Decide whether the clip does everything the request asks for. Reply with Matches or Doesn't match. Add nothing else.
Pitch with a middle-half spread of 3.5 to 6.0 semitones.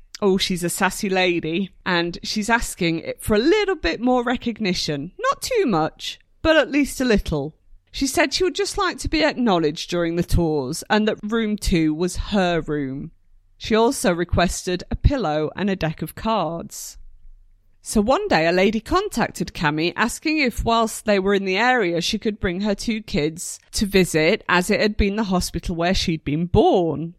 Matches